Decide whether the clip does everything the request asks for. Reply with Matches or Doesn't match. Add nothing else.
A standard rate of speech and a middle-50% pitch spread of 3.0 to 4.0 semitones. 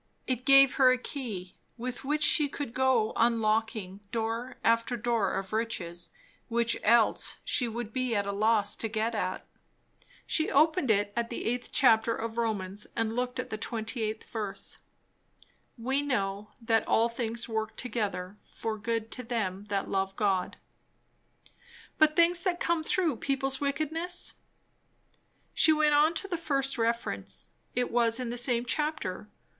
Matches